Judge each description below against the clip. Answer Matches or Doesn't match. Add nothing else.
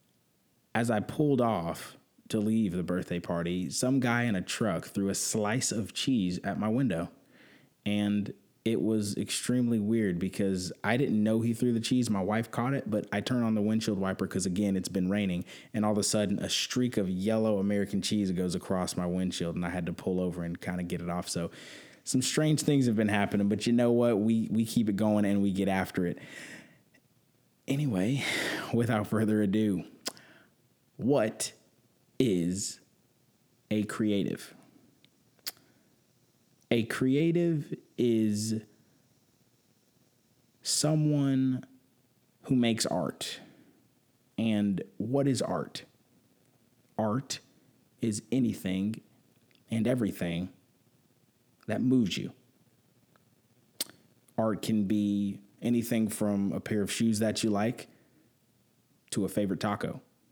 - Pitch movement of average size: Matches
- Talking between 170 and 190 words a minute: Doesn't match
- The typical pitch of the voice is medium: Doesn't match